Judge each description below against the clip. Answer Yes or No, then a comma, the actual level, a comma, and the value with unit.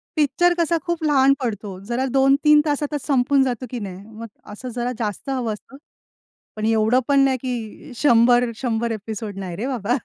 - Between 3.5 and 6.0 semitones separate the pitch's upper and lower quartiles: Yes, average, 3.8 semitones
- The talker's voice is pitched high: Yes, high, 245 Hz